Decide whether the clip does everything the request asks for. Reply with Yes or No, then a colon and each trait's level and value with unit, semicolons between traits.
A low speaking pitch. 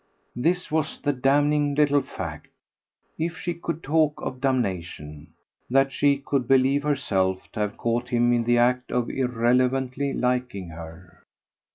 Yes: low, 125 Hz